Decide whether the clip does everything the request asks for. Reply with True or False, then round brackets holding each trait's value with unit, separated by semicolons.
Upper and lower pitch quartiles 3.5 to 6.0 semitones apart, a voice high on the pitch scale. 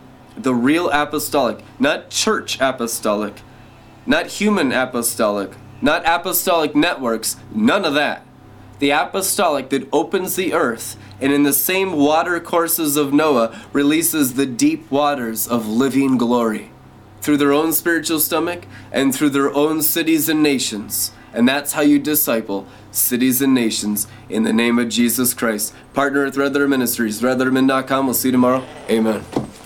False (4.2 semitones; 135 Hz)